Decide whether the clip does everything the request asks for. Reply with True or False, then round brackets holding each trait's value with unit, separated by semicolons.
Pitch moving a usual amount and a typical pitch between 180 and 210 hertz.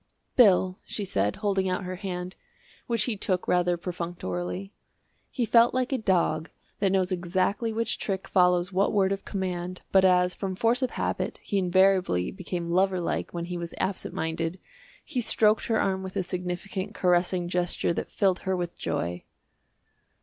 False (1.9 semitones; 185 Hz)